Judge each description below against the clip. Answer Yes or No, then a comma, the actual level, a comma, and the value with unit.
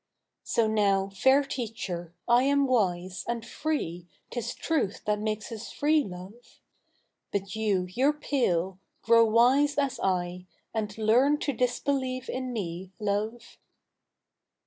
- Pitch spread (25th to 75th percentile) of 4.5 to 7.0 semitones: Yes, average, 4.9 semitones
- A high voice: Yes, high, 225 Hz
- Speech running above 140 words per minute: No, slow, 135 wpm